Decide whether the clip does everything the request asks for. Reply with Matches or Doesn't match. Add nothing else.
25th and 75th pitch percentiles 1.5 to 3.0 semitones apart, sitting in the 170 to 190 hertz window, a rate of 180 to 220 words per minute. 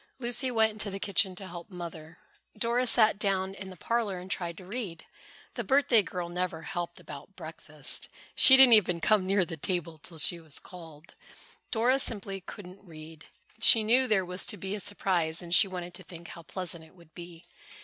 Doesn't match